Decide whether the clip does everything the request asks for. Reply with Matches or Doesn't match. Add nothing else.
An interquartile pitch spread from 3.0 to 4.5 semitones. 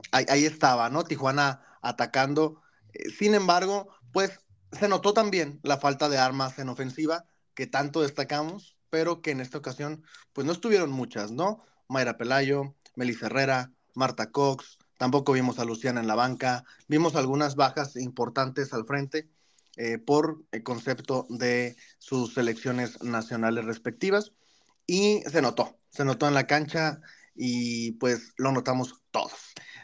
Matches